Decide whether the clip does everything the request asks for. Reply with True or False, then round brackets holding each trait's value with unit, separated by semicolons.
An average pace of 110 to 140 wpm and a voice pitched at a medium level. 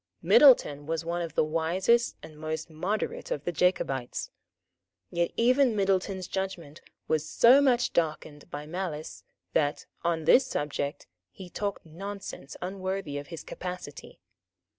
True (135 wpm; 175 Hz)